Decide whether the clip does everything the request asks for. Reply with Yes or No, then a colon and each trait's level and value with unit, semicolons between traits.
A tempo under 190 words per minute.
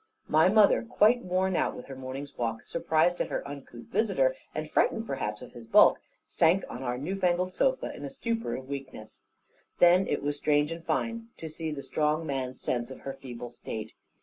No: average, 200 wpm